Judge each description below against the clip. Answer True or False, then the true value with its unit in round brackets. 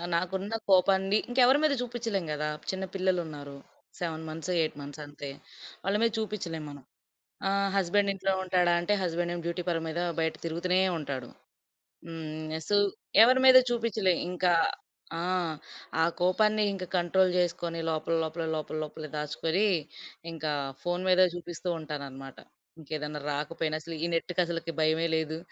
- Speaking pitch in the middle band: True (170 Hz)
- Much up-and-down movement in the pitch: False (3.3 semitones)